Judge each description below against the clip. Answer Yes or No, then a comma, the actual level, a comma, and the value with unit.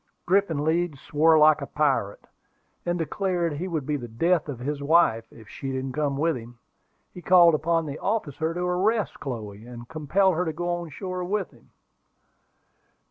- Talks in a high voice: No, medium, 155 Hz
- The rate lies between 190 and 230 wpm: No, average, 180 wpm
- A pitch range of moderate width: Yes, average, 4.3 semitones